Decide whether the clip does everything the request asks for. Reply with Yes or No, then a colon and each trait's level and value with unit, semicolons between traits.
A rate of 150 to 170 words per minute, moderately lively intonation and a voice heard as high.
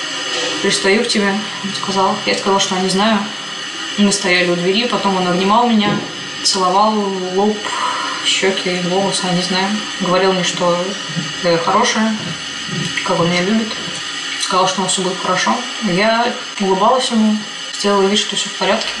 No: fast, 160 wpm; narrow, 1.9 semitones; high, 195 Hz